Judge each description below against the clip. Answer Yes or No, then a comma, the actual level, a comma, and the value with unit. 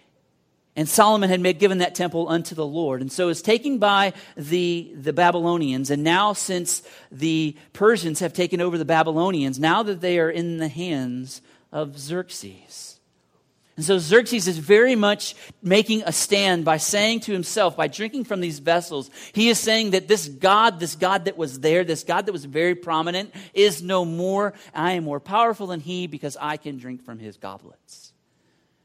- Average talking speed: Yes, average, 185 wpm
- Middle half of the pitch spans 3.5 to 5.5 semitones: Yes, average, 4.0 semitones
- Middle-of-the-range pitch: Yes, medium, 175 Hz